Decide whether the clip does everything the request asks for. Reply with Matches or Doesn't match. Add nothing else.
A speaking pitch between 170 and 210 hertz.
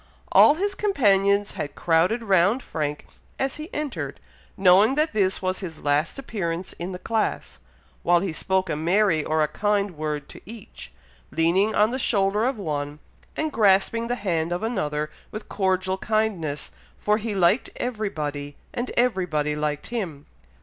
Matches